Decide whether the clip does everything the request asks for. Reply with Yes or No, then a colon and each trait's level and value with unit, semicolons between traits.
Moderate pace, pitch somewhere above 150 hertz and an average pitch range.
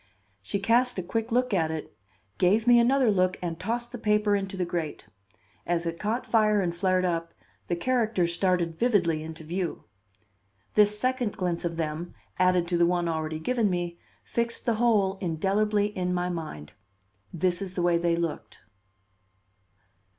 Yes: average, 165 wpm; medium, 185 Hz; average, 3.8 semitones